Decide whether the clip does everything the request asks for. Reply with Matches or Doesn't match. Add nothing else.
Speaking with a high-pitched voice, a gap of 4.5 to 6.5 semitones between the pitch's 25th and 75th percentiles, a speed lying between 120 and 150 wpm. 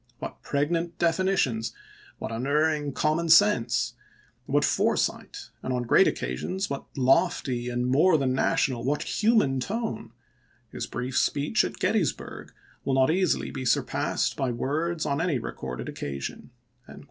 Doesn't match